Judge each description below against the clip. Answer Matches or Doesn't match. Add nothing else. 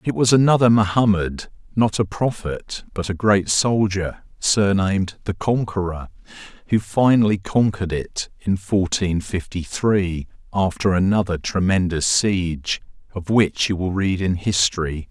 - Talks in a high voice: Doesn't match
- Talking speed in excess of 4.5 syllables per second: Doesn't match